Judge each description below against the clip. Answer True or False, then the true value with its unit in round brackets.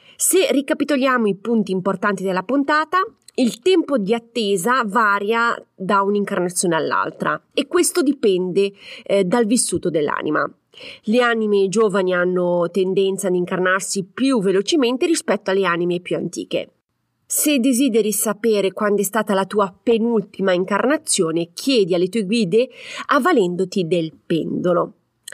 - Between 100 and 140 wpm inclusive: True (125 wpm)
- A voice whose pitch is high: True (205 Hz)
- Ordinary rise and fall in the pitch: True (4.6 semitones)